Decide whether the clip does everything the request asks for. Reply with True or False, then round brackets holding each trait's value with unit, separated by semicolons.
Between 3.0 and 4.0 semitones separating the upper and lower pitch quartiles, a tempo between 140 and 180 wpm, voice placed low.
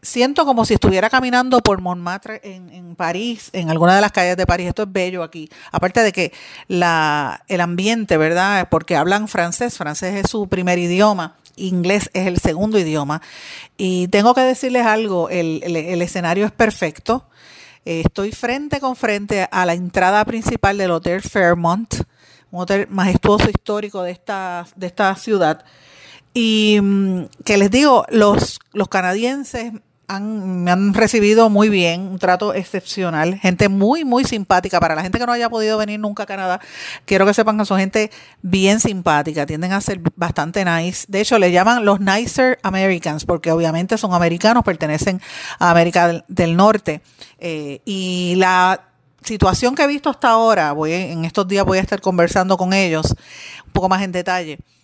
False (3.4 semitones; 170 wpm; 190 Hz)